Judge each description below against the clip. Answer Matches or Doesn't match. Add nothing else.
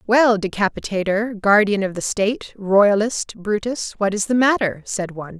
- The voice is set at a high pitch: Matches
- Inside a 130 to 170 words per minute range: Matches